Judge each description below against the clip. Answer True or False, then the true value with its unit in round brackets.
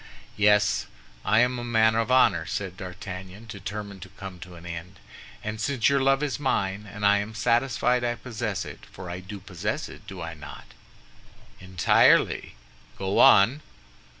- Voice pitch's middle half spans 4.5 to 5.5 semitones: False (4.1 semitones)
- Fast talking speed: False (160 wpm)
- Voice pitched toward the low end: True (105 Hz)